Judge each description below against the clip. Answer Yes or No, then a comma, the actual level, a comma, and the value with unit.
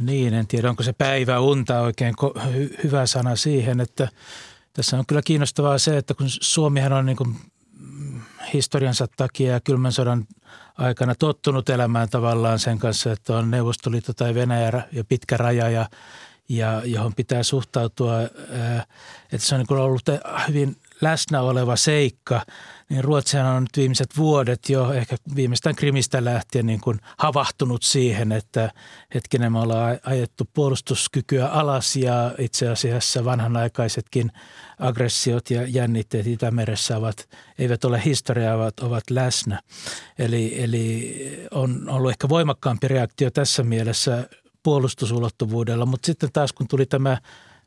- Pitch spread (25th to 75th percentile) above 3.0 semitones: No, narrow, 2.6 semitones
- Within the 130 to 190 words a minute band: Yes, average, 140 wpm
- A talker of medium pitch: No, low, 125 Hz